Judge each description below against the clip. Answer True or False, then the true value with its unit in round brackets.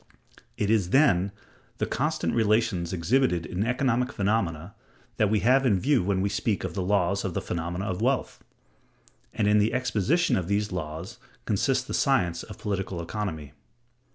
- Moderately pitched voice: False (100 Hz)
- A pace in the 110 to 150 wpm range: False (165 wpm)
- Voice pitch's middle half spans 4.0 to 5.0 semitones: True (4.4 semitones)